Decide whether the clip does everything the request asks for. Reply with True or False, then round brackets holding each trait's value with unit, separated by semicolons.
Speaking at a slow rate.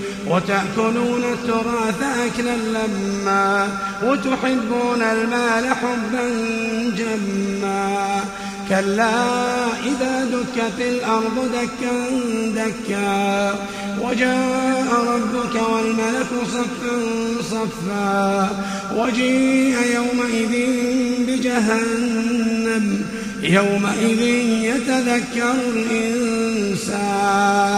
True (55 wpm)